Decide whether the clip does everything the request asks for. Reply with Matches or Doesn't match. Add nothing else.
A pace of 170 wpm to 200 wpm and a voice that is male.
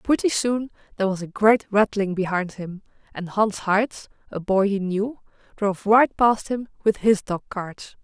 Doesn't match